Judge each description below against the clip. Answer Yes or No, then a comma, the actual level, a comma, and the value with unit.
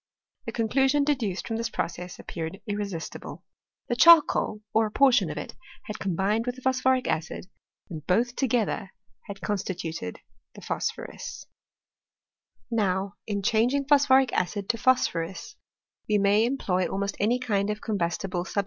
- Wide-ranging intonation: No, average, 4.5 semitones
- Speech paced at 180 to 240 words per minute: No, average, 140 wpm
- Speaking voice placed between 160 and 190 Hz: No, high, 210 Hz